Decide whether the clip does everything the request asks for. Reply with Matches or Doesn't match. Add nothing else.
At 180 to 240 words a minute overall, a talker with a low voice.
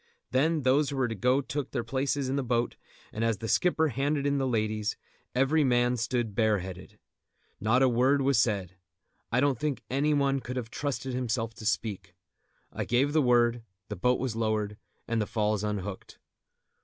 Matches